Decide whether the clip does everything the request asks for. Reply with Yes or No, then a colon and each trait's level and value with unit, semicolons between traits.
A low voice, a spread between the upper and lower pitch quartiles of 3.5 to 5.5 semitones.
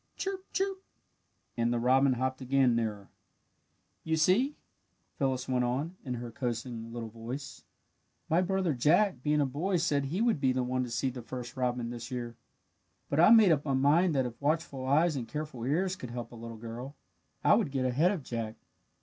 Yes: low, 130 Hz; average, 4.8 semitones